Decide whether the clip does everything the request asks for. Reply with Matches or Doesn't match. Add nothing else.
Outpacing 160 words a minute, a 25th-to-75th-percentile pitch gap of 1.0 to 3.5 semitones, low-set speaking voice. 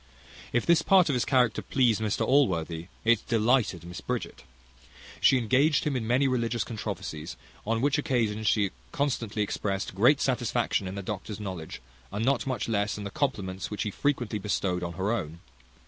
Doesn't match